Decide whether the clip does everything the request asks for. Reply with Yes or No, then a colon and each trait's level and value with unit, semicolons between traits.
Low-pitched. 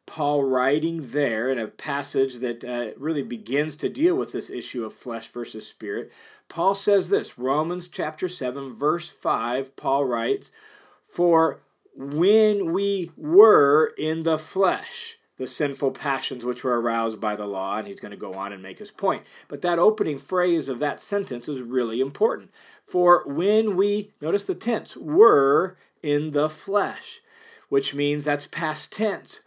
No: medium, 155 Hz